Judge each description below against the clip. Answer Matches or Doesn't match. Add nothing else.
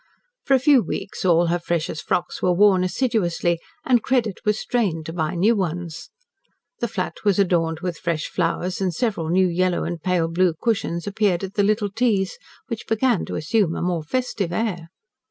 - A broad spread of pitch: Doesn't match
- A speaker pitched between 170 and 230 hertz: Matches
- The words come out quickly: Doesn't match